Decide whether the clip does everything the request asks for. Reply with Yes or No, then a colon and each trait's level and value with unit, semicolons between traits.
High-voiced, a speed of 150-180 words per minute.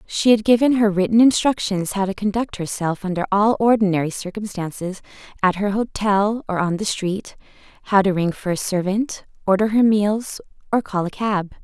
Yes: high, 200 Hz; average, 170 wpm